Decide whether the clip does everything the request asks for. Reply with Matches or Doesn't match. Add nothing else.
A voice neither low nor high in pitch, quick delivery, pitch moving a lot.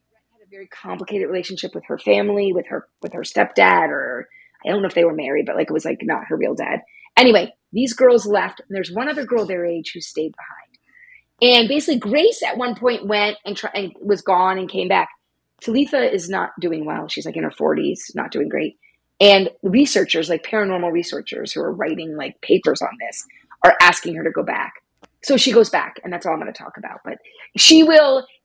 Doesn't match